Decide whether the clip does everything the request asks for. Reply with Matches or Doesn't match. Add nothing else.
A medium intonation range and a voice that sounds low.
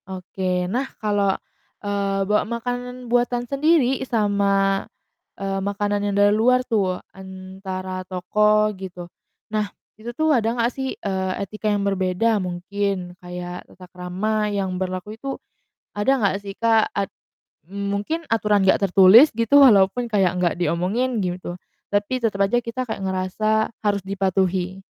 Doesn't match